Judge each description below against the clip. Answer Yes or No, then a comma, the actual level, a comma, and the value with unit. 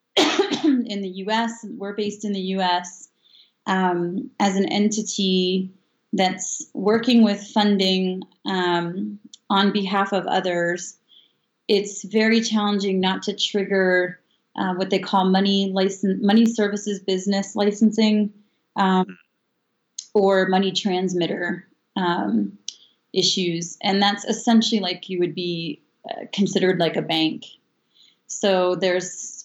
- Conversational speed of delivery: No, slow, 115 wpm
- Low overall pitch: No, high, 195 Hz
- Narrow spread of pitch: Yes, narrow, 2.3 semitones